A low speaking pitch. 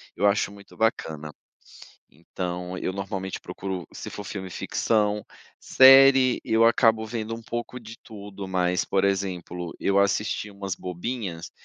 Yes: low, 100 Hz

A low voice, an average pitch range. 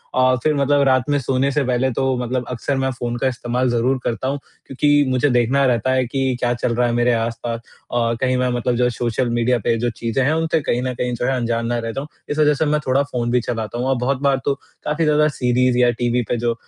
No: low, 125 Hz; narrow, 2.0 semitones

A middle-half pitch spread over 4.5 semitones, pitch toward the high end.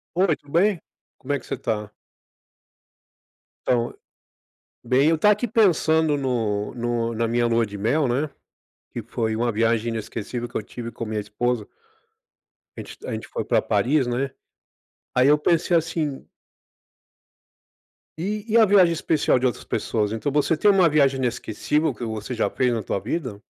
No: wide, 5.5 semitones; low, 125 Hz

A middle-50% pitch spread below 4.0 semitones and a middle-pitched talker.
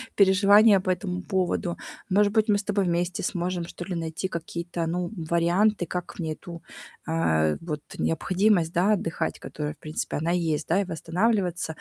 Yes: average, 2.8 semitones; medium, 175 Hz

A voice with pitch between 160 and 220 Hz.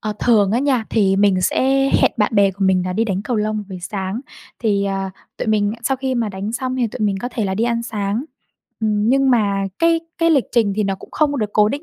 Yes: high, 215 Hz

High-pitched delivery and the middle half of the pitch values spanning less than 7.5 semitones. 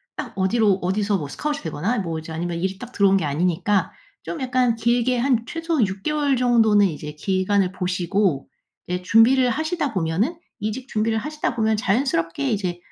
Yes: high, 210 Hz; wide, 5.5 semitones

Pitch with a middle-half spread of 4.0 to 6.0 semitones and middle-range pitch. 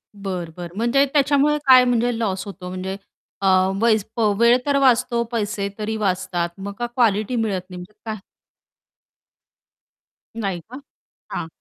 No: average, 4.4 semitones; high, 215 Hz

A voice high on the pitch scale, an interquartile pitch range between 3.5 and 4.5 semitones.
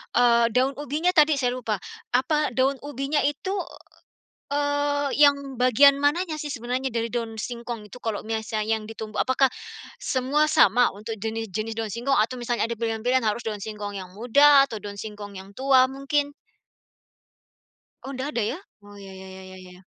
Yes: high, 245 Hz; average, 4.2 semitones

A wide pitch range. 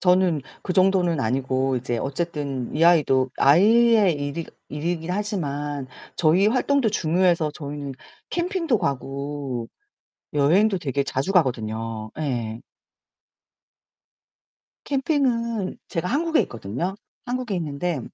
Yes: wide, 6.3 semitones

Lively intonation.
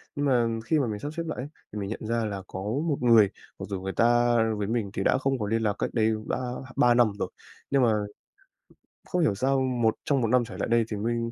No: average, 3.4 semitones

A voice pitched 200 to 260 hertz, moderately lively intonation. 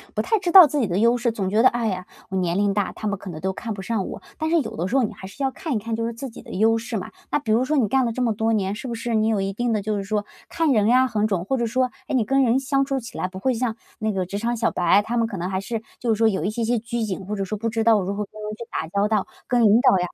Yes: high, 220 Hz; average, 3.2 semitones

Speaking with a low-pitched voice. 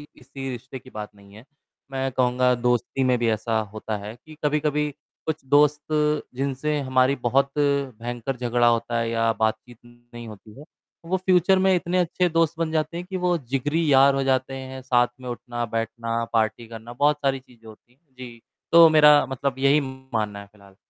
Yes: low, 130 Hz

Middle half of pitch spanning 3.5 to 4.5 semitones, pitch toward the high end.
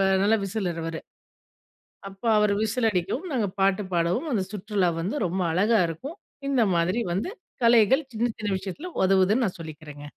Yes: average, 4.2 semitones; high, 200 Hz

